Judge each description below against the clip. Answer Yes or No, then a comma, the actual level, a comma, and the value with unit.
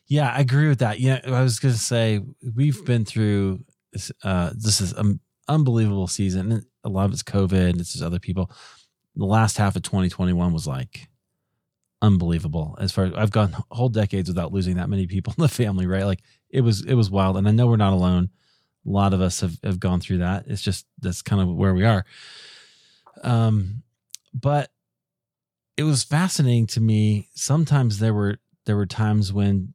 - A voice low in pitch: Yes, low, 105 Hz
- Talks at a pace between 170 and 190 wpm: No, average, 200 wpm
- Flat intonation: No, average, 4.3 semitones